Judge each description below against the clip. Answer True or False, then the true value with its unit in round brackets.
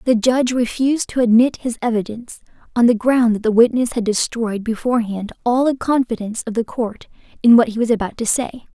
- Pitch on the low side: False (235 Hz)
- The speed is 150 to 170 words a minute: False (200 wpm)